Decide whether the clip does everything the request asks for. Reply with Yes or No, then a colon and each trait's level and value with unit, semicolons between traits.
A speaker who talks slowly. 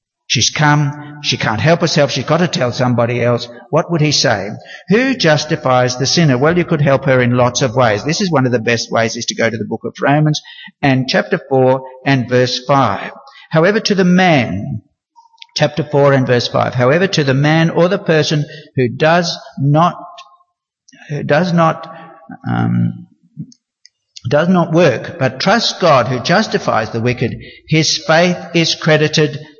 No: average, 175 wpm